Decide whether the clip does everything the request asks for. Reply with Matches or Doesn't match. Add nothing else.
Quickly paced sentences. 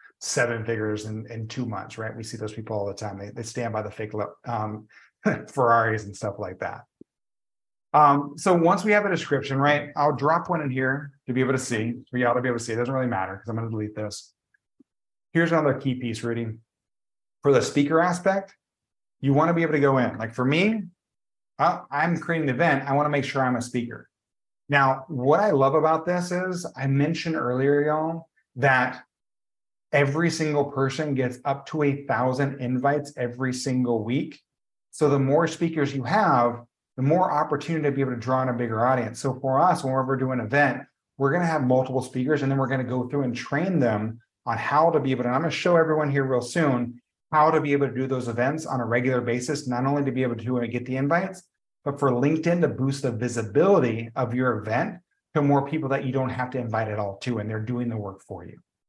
Matches